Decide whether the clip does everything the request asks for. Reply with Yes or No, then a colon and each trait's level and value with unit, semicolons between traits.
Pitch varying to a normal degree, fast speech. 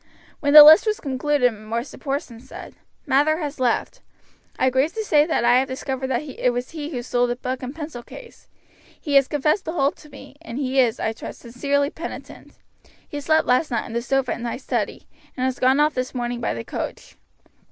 Yes: average, 3.2 semitones; fast, 215 wpm